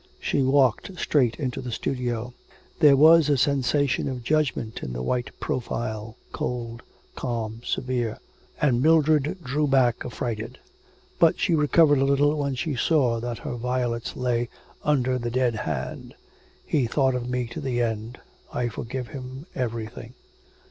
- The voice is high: No, low, 125 Hz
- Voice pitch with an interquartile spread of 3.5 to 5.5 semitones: No, average, 3.1 semitones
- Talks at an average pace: Yes, average, 150 wpm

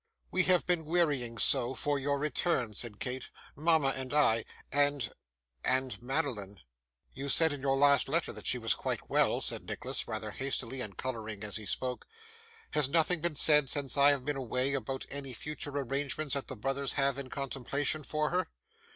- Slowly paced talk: No, average, 180 wpm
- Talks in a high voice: No, medium, 140 Hz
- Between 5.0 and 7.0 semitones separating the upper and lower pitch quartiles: No, narrow, 2.4 semitones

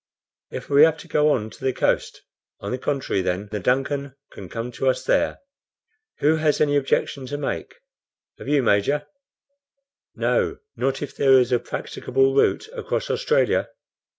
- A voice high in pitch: No, low, 135 Hz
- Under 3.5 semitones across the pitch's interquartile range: Yes, average, 2.9 semitones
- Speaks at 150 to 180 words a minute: Yes, average, 165 wpm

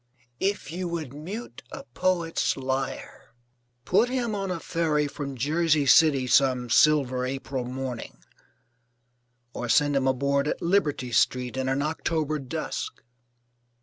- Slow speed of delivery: Yes, slow, 130 wpm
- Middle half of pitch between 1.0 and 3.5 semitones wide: No, average, 4.1 semitones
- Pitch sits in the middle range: Yes, medium, 145 Hz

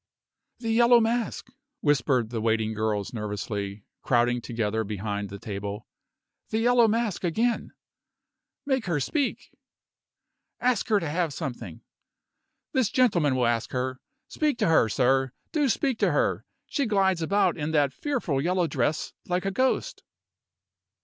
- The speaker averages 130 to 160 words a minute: Yes, average, 140 wpm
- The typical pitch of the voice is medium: Yes, medium, 150 Hz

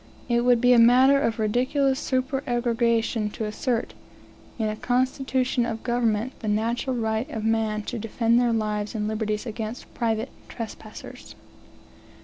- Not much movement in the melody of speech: Yes, narrow, 2.2 semitones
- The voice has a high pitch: Yes, high, 230 Hz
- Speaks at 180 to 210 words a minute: No, average, 140 wpm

